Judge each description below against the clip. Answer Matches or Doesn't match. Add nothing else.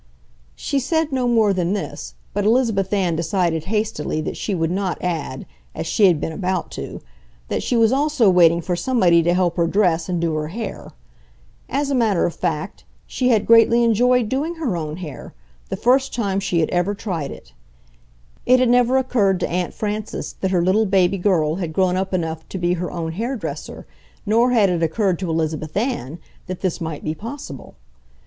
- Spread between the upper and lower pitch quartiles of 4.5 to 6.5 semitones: Matches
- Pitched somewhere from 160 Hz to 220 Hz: Matches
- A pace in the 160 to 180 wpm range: Doesn't match